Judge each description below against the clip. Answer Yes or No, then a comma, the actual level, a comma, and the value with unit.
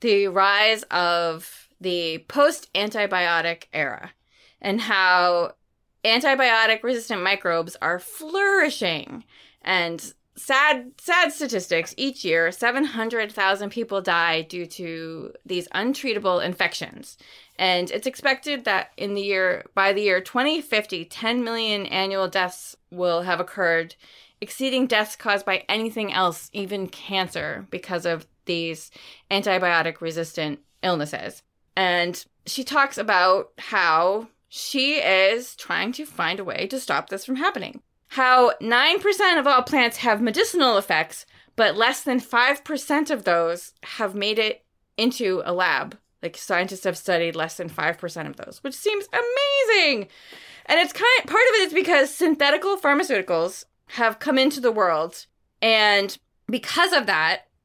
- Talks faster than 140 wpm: No, slow, 135 wpm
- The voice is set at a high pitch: Yes, high, 205 Hz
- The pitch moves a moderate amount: No, wide, 6.8 semitones